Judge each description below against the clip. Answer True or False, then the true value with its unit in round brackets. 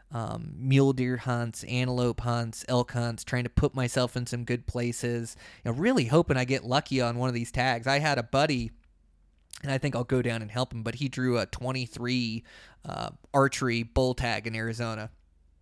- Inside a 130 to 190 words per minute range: False (205 wpm)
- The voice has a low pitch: True (120 Hz)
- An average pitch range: False (1.9 semitones)